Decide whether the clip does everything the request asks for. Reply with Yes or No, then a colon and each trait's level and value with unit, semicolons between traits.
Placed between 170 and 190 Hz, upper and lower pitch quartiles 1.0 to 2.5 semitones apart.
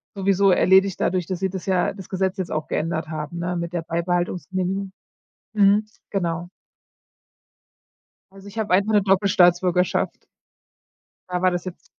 Yes: medium, 185 Hz; narrow, 1.8 semitones